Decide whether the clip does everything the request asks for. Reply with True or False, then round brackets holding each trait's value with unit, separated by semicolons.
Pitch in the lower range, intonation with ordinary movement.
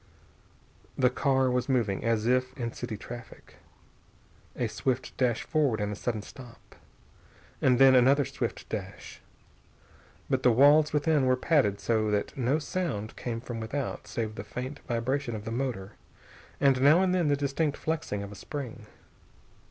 True (125 Hz; 3.6 semitones)